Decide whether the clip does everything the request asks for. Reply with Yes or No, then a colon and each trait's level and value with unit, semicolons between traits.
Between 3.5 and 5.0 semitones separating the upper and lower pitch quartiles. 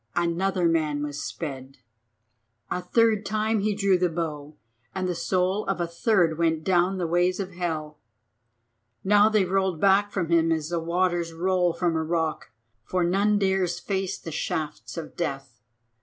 No: average, 2.9 semitones